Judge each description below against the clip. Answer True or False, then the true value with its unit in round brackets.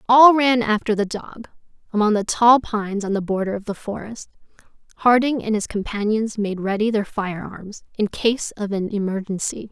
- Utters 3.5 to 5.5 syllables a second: True (5.0 syllables/s)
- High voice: True (215 Hz)